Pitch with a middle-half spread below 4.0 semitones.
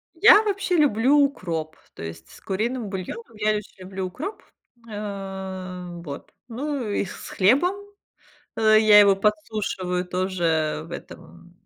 No: average, 4.3 semitones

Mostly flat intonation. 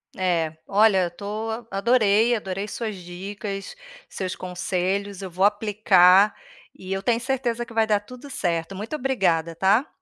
No: average, 3.2 semitones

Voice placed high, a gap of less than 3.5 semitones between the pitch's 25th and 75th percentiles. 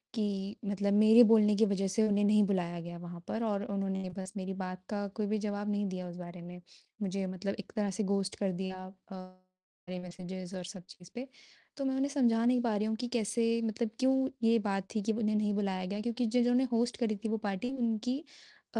Yes: high, 205 Hz; average, 3.1 semitones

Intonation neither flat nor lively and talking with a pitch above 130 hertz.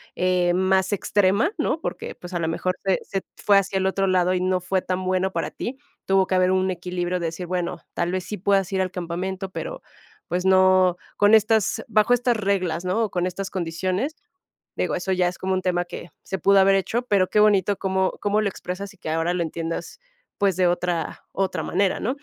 No: narrow, 1.6 semitones; medium, 185 Hz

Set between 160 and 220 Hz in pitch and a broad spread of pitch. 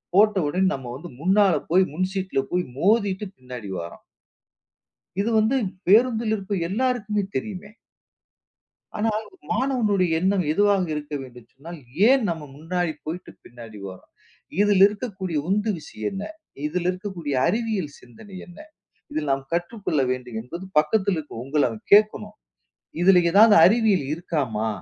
Yes: medium, 185 Hz; wide, 5.7 semitones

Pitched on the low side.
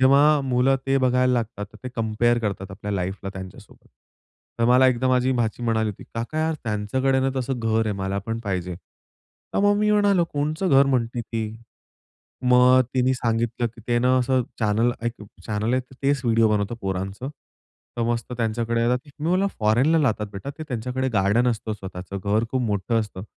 Yes: low, 120 Hz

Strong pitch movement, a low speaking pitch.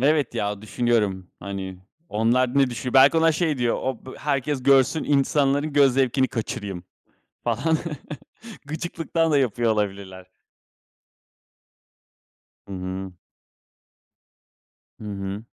Yes: wide, 5.8 semitones; low, 125 Hz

